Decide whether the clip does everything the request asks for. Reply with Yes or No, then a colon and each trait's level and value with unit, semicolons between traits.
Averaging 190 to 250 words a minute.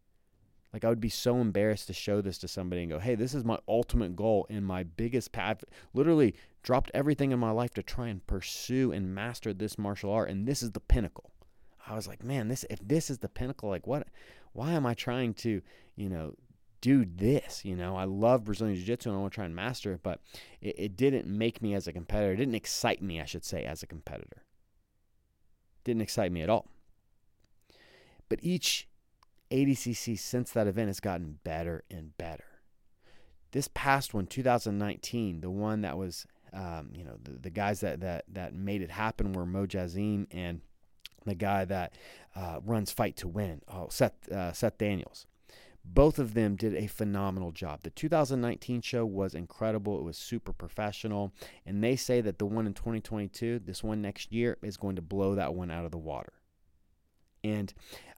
Yes: average, 200 wpm